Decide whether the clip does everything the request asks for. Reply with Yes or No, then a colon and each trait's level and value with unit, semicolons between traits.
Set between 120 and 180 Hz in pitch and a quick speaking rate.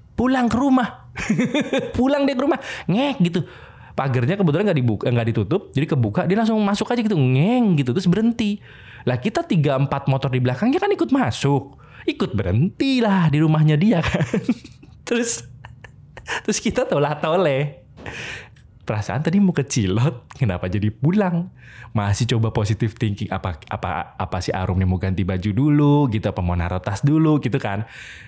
Yes: medium, 140 Hz; fast, 160 wpm